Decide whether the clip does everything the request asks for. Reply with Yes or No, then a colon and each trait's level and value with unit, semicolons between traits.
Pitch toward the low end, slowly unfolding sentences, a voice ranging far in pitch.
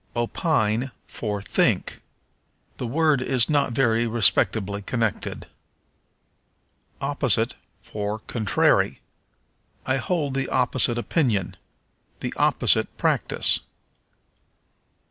No: low, 120 Hz; slow, 85 wpm; average, 3.8 semitones